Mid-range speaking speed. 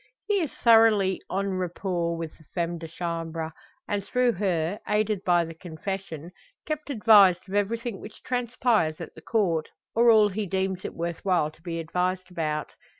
Yes: average, 170 wpm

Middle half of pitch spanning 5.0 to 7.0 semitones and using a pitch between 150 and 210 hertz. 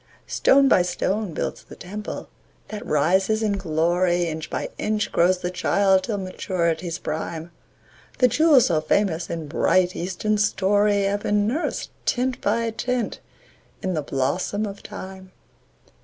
No: average, 3.4 semitones; high, 190 Hz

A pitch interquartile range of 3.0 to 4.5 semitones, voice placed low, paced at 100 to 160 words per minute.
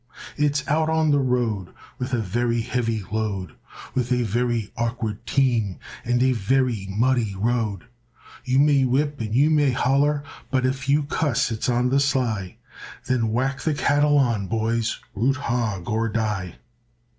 Yes: average, 3.7 semitones; low, 120 Hz; average, 155 wpm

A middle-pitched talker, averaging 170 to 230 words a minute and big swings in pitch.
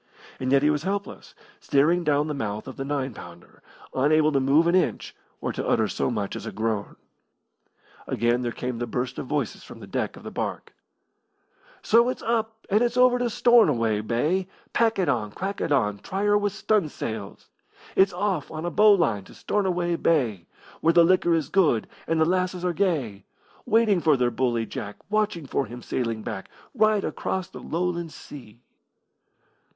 Yes: medium, 155 Hz; average, 185 wpm; wide, 8.0 semitones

